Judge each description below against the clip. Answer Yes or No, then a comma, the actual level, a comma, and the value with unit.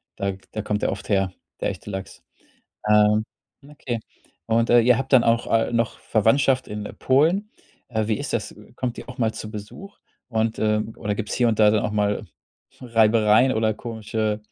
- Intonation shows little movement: Yes, narrow, 2.3 semitones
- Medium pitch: No, low, 110 Hz